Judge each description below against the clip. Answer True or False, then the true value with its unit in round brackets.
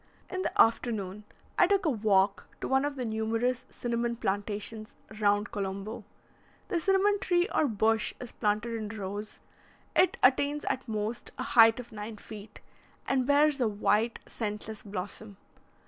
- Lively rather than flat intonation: False (3.5 semitones)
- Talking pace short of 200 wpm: True (150 wpm)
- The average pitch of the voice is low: False (225 Hz)